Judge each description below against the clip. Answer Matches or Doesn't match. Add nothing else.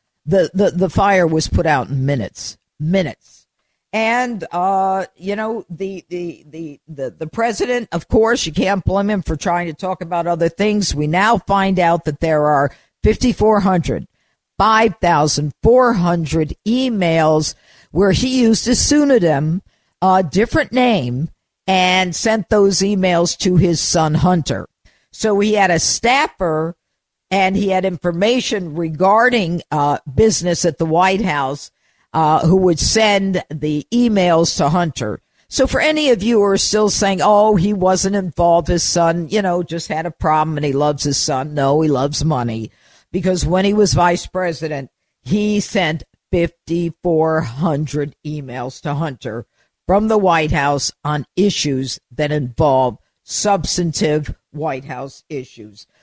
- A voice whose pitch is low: Doesn't match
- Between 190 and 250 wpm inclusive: Doesn't match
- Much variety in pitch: Doesn't match